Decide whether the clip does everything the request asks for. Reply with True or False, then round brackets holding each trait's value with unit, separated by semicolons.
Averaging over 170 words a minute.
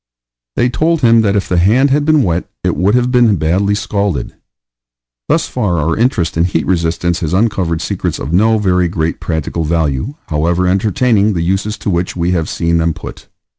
True (190 wpm)